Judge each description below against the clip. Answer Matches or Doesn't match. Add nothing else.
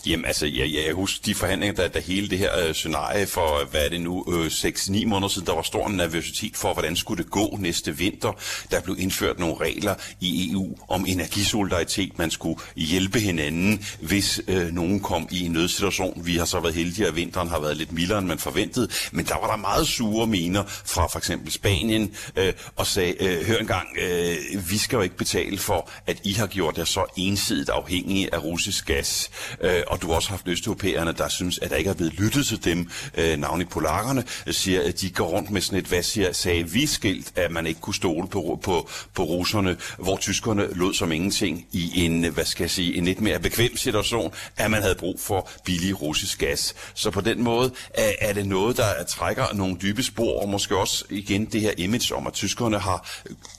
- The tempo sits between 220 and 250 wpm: Doesn't match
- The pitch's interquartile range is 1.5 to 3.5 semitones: Matches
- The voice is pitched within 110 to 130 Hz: Doesn't match